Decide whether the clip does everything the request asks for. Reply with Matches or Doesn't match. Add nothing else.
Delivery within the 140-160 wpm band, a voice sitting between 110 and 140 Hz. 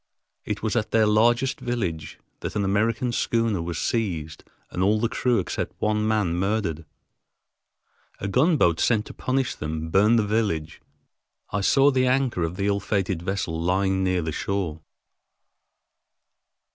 Doesn't match